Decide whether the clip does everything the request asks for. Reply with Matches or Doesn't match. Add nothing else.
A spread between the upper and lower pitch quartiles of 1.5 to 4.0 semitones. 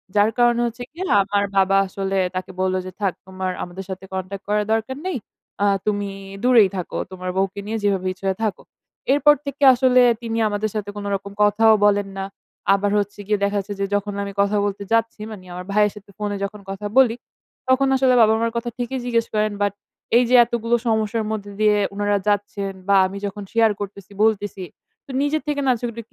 Matches